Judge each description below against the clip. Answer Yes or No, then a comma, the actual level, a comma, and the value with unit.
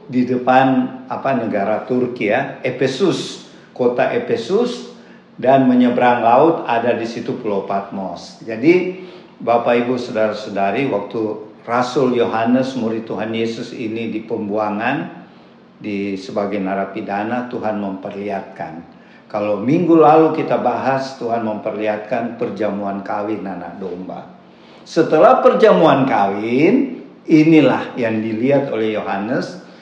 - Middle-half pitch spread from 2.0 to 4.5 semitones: Yes, average, 3.1 semitones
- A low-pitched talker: Yes, low, 115 Hz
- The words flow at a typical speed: Yes, average, 110 wpm